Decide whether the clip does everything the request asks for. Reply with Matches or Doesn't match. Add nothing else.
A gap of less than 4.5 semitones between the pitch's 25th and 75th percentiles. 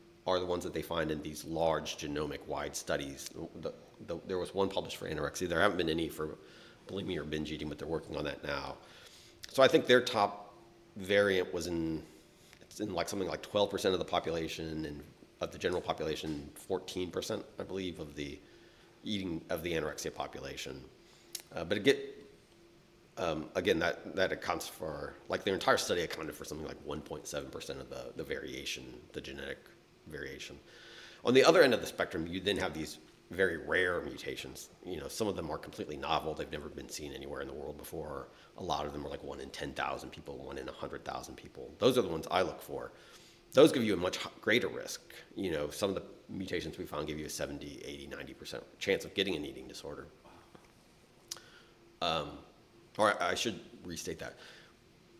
Matches